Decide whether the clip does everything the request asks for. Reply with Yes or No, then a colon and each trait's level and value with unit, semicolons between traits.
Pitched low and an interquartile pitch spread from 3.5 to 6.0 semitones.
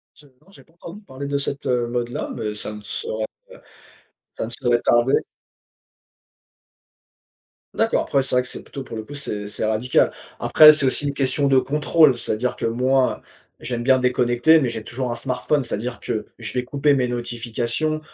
No: low, 125 Hz; average, 2.9 semitones